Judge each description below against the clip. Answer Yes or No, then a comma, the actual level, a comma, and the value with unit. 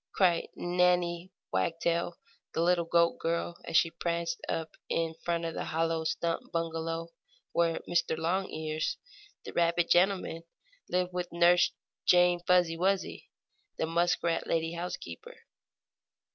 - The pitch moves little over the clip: Yes, narrow, 1.2 semitones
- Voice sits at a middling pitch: Yes, medium, 170 Hz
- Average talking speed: No, slow, 125 wpm